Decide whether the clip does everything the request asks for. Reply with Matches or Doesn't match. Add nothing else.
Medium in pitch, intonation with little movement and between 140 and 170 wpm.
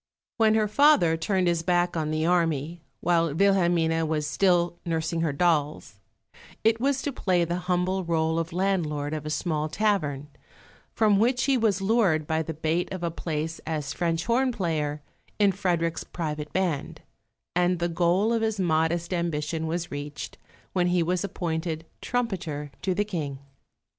Doesn't match